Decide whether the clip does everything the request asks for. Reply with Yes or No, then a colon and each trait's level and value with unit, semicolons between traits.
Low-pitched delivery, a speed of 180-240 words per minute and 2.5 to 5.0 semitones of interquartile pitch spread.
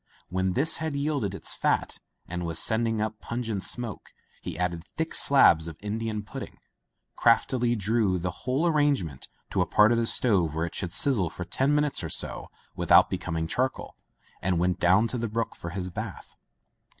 No: low, 105 Hz; average, 190 wpm; wide, 5.6 semitones